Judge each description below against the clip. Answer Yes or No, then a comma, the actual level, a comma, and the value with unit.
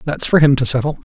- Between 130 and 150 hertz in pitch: Yes, medium, 140 Hz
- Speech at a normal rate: No, fast, 270 wpm